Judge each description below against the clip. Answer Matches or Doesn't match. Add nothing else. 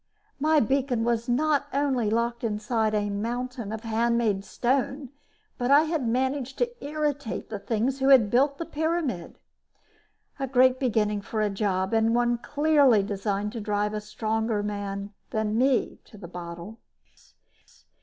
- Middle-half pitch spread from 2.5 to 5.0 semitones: Matches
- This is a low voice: Doesn't match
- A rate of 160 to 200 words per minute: Doesn't match